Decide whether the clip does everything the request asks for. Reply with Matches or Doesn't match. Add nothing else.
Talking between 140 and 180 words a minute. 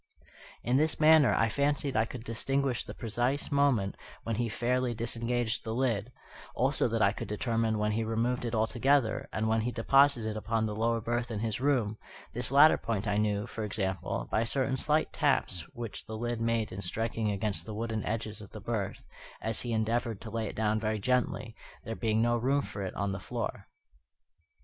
Doesn't match